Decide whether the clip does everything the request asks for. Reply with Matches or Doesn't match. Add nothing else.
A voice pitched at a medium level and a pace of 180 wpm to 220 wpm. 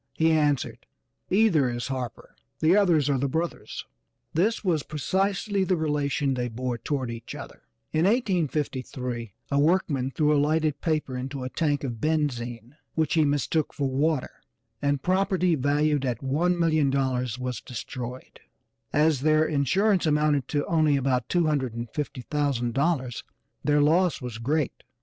Doesn't match